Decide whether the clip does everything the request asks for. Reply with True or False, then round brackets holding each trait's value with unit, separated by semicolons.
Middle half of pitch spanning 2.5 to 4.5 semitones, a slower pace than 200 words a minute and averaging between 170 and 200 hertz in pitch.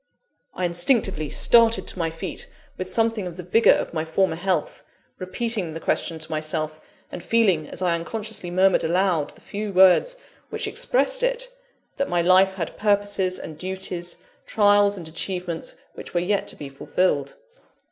True (3.3 semitones; 165 wpm; 185 Hz)